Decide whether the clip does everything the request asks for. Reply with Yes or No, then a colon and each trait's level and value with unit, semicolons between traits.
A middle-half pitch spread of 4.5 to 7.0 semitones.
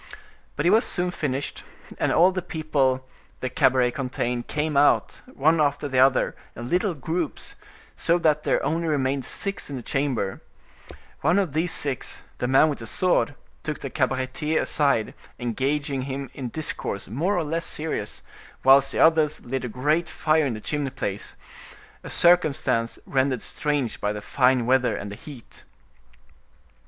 No: average, 3.5 semitones